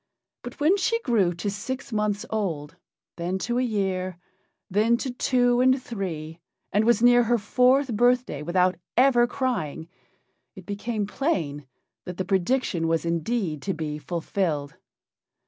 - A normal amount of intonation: No, wide, 6.1 semitones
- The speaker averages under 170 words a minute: Yes, average, 145 wpm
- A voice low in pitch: No, high, 205 Hz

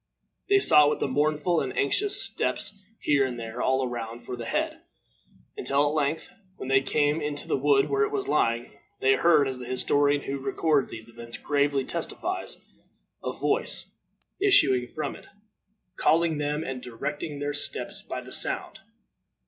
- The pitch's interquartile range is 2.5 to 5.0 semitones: Yes, average, 2.9 semitones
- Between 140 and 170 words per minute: Yes, average, 165 wpm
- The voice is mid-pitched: Yes, medium, 145 Hz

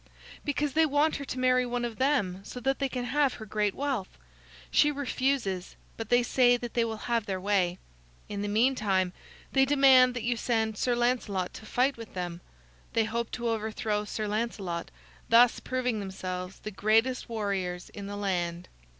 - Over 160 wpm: Yes, average, 180 wpm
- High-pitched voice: Yes, high, 230 Hz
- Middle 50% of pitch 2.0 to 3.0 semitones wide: No, average, 4.0 semitones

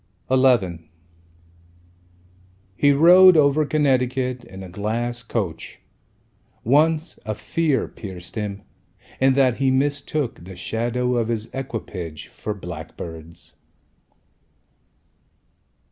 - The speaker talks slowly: Yes, slow, 95 wpm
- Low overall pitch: Yes, low, 120 Hz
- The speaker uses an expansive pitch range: Yes, wide, 5.7 semitones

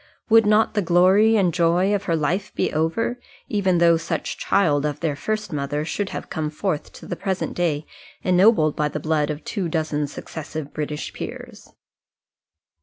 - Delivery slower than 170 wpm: No, average, 175 wpm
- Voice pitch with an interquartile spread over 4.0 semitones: Yes, average, 4.6 semitones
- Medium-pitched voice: Yes, medium, 170 Hz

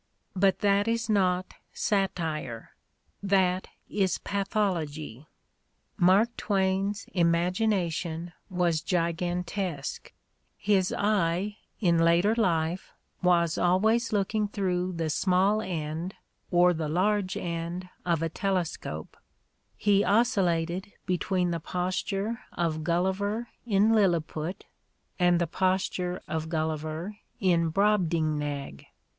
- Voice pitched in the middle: Yes, medium, 180 Hz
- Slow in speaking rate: Yes, slow, 100 wpm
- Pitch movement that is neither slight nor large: Yes, average, 3.1 semitones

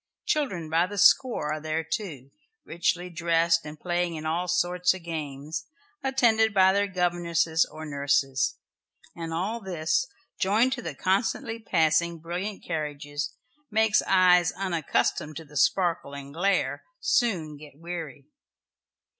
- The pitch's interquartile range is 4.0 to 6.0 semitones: No, average, 3.5 semitones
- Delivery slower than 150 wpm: Yes, slow, 135 wpm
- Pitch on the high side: No, medium, 170 Hz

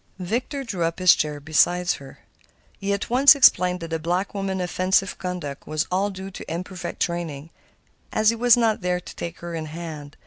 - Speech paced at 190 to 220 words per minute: Yes, average, 195 wpm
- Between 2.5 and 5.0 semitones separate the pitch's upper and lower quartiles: Yes, average, 3.1 semitones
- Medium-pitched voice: Yes, medium, 180 Hz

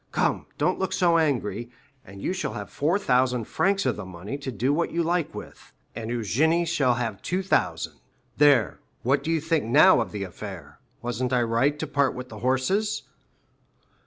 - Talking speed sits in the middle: Yes, average, 180 wpm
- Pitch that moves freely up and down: Yes, wide, 6.1 semitones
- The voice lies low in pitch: Yes, low, 130 Hz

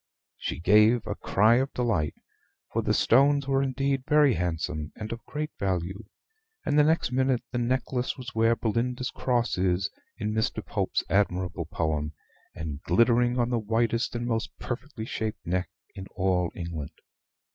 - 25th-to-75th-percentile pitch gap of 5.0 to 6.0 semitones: Yes, wide, 5.4 semitones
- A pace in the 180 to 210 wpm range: No, average, 155 wpm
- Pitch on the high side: No, low, 115 Hz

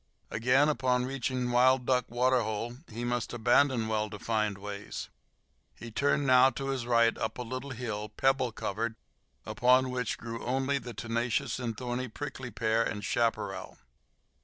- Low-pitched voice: Yes, low, 120 Hz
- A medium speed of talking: Yes, average, 150 wpm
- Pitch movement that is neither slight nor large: No, narrow, 2.2 semitones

